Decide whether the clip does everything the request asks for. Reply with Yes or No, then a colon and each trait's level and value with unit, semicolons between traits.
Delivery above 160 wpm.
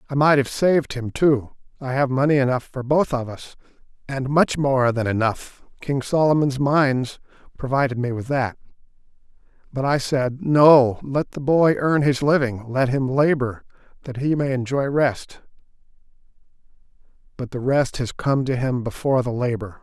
No: average, 155 wpm